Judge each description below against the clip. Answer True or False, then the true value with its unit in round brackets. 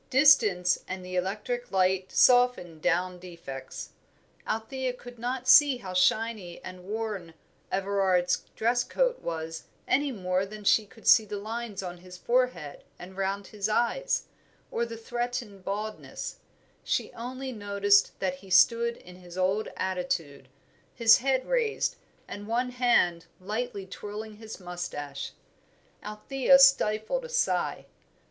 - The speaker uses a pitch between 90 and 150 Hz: False (210 Hz)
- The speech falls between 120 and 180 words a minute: True (135 wpm)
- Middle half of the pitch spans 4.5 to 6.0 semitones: True (4.8 semitones)